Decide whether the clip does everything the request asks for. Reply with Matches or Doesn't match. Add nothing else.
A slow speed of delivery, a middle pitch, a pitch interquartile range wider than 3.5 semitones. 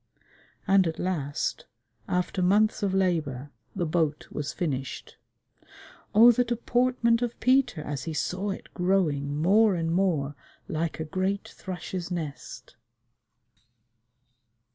Matches